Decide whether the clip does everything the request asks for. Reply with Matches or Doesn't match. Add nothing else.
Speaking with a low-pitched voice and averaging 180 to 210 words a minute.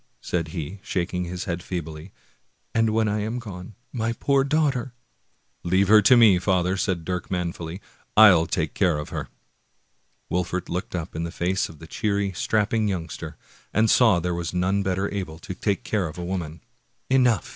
Matches